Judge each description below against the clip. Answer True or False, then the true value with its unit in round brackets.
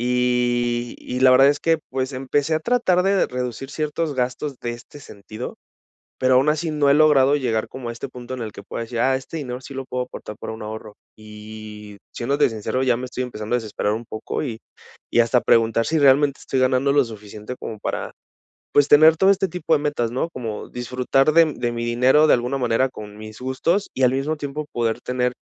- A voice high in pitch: False (125 Hz)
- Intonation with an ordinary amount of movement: True (3.5 semitones)